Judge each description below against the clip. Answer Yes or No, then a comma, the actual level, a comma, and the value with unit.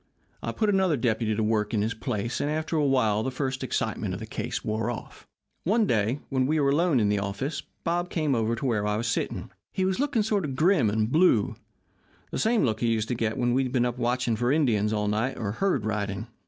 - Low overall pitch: Yes, low, 120 Hz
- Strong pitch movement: Yes, wide, 5.8 semitones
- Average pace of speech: No, fast, 235 wpm